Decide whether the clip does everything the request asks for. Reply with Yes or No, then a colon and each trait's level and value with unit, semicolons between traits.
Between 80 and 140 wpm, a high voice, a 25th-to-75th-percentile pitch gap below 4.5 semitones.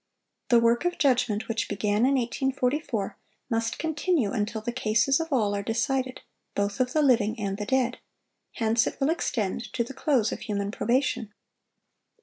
No: average, 165 wpm; high, 235 Hz; average, 3.8 semitones